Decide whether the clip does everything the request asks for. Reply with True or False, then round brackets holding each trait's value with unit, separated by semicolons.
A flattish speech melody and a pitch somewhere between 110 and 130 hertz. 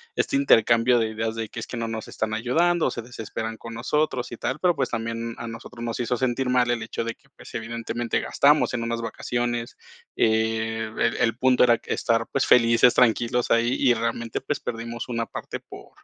True (1.5 semitones; 115 Hz)